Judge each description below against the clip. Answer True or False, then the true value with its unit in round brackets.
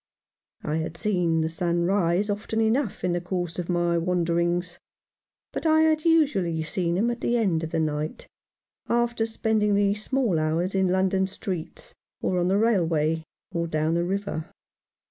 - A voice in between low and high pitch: True (180 Hz)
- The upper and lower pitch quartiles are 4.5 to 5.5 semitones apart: False (3.8 semitones)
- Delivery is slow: False (170 wpm)